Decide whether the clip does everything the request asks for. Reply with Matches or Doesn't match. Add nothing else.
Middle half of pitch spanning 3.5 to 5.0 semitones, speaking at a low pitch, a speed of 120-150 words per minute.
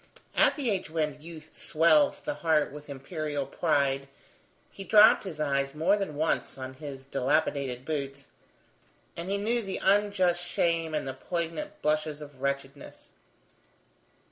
Doesn't match